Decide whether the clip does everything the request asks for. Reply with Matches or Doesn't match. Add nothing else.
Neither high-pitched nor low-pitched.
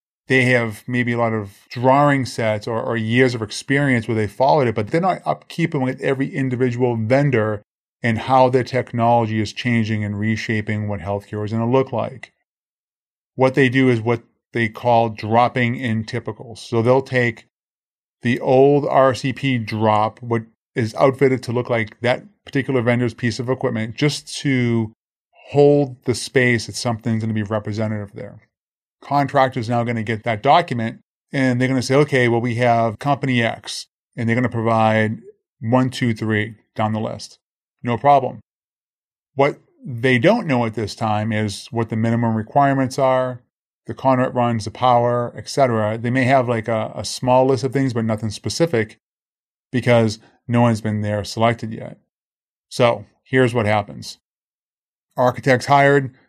Doesn't match